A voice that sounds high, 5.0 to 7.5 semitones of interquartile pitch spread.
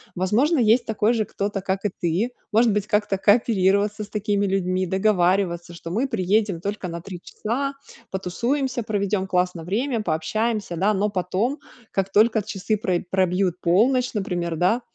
No: high, 200 Hz; average, 3.1 semitones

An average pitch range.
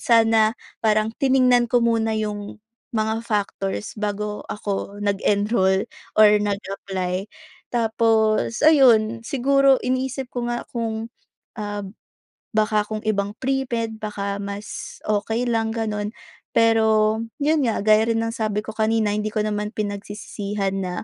No: narrow, 1.8 semitones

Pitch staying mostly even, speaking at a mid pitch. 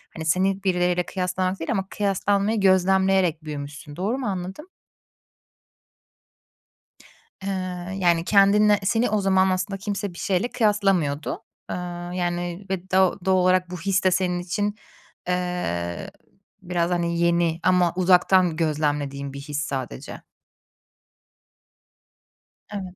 Yes: narrow, 2.2 semitones; medium, 180 Hz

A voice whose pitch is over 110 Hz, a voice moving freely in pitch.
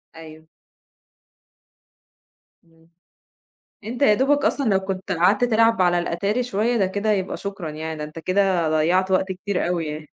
No: high, 190 Hz; average, 4.3 semitones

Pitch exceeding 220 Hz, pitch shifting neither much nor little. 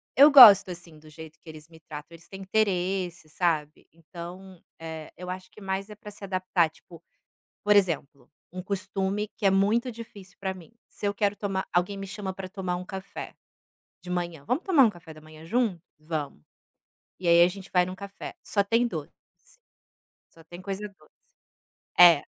No: medium, 185 Hz; average, 3.1 semitones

